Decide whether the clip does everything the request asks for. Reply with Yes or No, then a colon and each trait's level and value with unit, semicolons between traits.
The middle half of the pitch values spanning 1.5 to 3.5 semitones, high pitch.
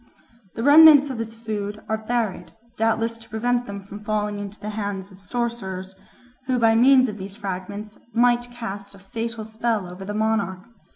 Yes: average, 2.7 semitones; high, 220 Hz